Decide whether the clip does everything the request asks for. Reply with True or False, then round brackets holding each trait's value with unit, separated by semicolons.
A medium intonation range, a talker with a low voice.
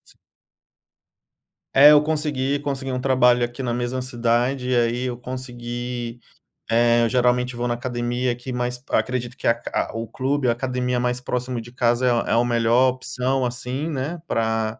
False (1.3 semitones; 125 Hz)